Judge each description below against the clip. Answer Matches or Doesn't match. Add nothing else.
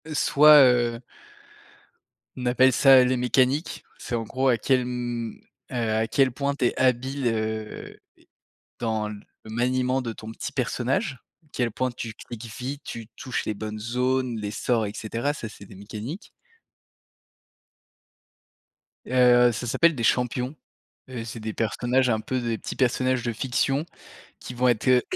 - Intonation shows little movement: Matches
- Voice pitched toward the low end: Matches